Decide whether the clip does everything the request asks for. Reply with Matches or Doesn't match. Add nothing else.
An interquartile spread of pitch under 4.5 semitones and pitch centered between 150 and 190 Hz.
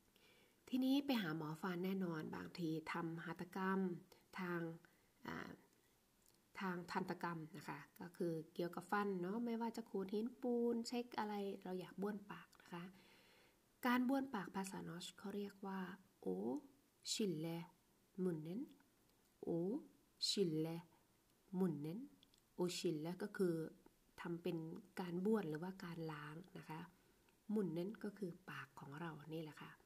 Matches